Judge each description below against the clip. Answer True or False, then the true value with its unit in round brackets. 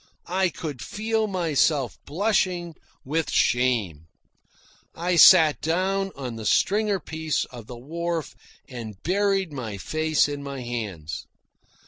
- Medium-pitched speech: True (155 Hz)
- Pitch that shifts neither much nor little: False (6.8 semitones)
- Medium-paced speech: False (120 wpm)